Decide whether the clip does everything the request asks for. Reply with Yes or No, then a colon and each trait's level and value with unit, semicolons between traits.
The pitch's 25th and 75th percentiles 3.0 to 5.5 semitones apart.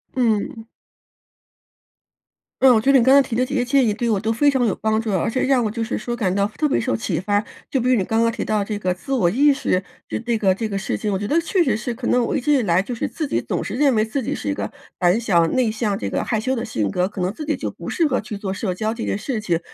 Yes: average, 4.2 semitones